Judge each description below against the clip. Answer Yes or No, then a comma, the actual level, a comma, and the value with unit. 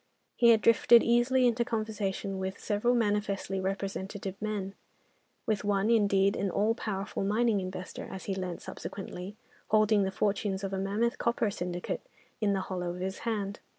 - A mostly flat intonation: Yes, narrow, 2.3 semitones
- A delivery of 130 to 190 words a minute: Yes, average, 160 wpm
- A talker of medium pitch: No, high, 200 Hz